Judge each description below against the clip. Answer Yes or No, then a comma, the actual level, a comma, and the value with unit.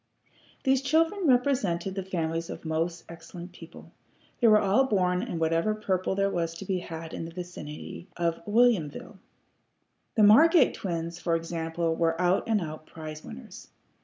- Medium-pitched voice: Yes, medium, 175 Hz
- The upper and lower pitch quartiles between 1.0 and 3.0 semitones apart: No, average, 4.2 semitones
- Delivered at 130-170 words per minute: Yes, average, 160 wpm